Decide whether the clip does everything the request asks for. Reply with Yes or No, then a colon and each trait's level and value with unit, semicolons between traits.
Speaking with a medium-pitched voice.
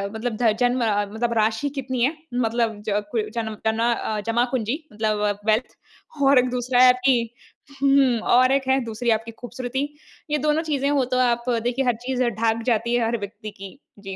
No: high, 240 Hz